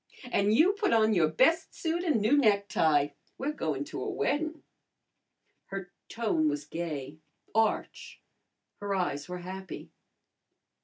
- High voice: Yes, high, 200 Hz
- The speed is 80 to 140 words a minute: Yes, slow, 135 wpm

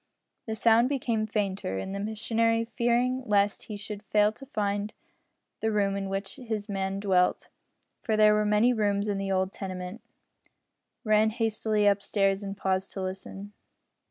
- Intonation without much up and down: Yes, narrow, 2.0 semitones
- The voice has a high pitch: Yes, high, 210 Hz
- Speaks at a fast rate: No, average, 160 wpm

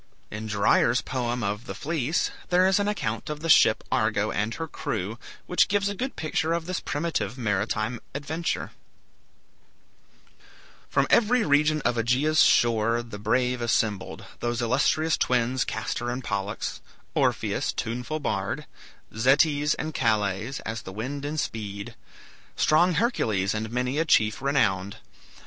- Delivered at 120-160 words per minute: Yes, average, 140 wpm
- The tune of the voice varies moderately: No, wide, 6.0 semitones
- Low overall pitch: Yes, low, 125 Hz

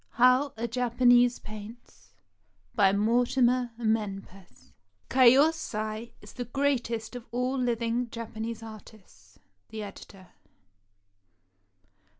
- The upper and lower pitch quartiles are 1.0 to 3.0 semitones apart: Yes, narrow, 2.5 semitones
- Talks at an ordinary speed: No, slow, 90 wpm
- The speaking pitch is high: Yes, high, 230 Hz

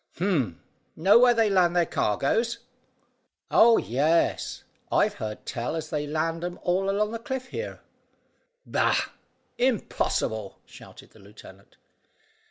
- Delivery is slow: Yes, slow, 125 wpm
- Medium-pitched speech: Yes, medium, 175 Hz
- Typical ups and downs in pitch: No, wide, 8.3 semitones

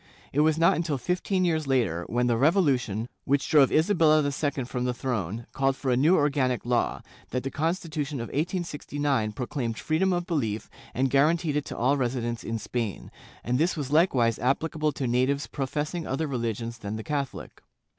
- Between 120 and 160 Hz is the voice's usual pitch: Yes, low, 135 Hz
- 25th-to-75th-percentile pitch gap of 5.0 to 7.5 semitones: No, average, 4.2 semitones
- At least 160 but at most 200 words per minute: Yes, average, 185 wpm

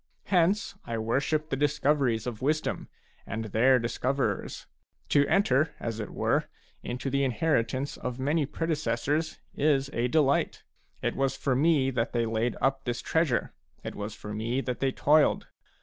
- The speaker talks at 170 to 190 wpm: No, average, 160 wpm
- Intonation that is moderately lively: Yes, average, 4.0 semitones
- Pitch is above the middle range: No, low, 135 Hz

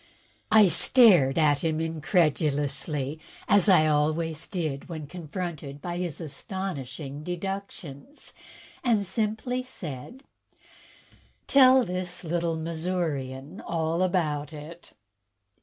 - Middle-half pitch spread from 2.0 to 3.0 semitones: No, average, 3.8 semitones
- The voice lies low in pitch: No, medium, 165 Hz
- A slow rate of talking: Yes, slow, 95 wpm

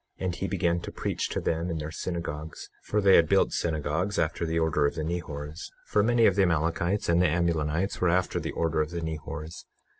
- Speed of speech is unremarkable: No, fast, 215 wpm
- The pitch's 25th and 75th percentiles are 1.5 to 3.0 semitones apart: Yes, narrow, 2.4 semitones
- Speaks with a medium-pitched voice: No, very low, 85 Hz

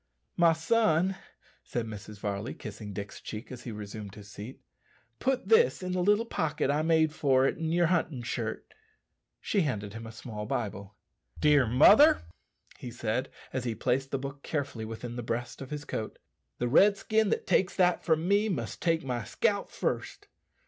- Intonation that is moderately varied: No, wide, 7.0 semitones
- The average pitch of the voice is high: No, low, 135 Hz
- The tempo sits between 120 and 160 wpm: No, average, 180 wpm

